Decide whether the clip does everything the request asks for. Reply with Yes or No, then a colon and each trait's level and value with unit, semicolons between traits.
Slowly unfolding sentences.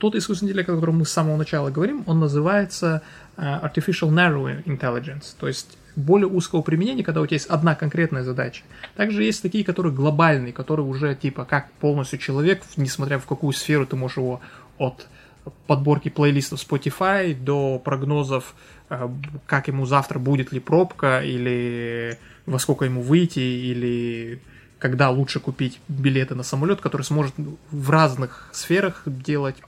No: average, 155 wpm